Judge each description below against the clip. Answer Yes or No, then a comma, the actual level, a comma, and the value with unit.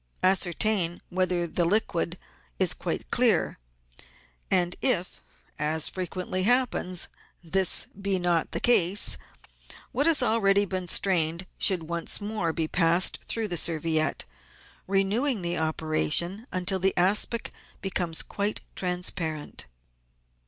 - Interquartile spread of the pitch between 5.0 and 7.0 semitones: No, average, 2.7 semitones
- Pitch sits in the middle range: Yes, medium, 180 Hz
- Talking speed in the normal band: No, slow, 115 wpm